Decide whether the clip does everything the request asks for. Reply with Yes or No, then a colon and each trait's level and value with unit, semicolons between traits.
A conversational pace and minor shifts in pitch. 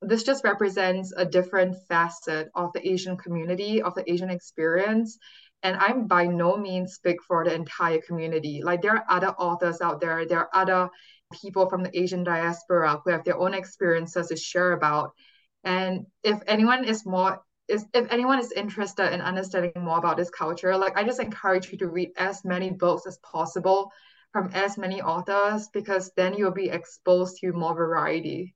Yes: average, 185 wpm; narrow, 2.2 semitones